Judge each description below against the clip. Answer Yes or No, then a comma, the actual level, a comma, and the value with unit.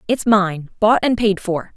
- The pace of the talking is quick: No, average, 170 wpm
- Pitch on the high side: Yes, high, 205 Hz